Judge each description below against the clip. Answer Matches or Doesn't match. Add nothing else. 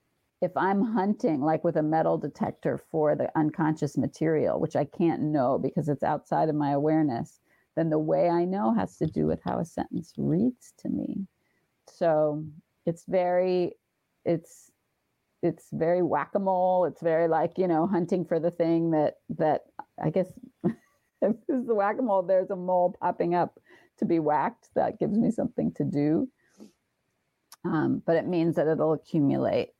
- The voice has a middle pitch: Matches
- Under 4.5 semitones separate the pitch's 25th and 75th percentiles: Matches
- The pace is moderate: Matches